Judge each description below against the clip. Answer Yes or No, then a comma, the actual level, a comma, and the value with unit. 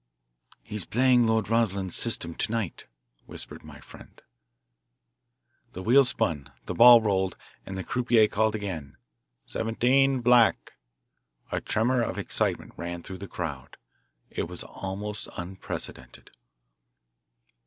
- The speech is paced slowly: Yes, slow, 120 wpm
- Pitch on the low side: Yes, low, 105 Hz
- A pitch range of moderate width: Yes, average, 4.0 semitones